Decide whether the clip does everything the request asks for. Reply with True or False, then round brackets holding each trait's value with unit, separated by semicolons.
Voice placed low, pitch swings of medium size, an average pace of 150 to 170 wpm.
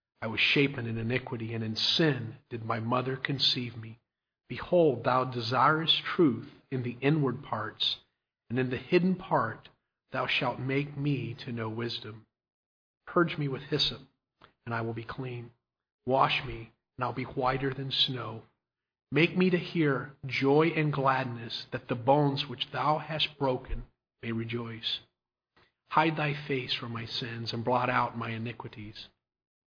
True (130 Hz; 3.3 semitones; 160 wpm)